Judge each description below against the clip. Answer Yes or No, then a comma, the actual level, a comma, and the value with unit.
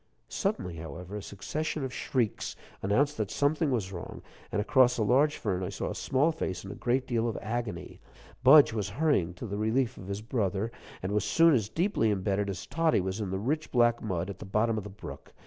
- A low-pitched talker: Yes, low, 110 Hz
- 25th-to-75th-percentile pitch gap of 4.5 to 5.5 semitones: Yes, average, 5.1 semitones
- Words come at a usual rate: No, fast, 215 wpm